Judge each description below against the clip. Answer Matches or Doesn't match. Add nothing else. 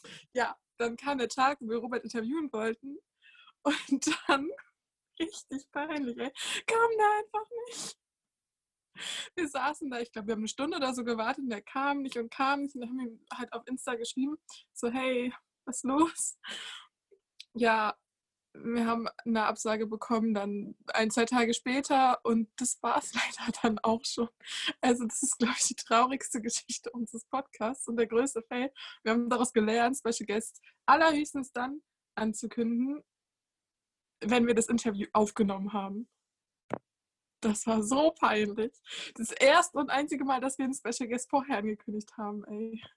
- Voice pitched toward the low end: Doesn't match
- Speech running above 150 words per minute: Matches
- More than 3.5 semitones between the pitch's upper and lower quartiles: Doesn't match